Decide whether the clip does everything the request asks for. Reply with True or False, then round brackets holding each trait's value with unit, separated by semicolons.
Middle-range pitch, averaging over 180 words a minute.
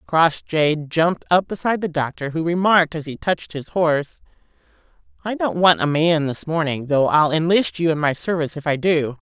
True (160 Hz; 195 wpm)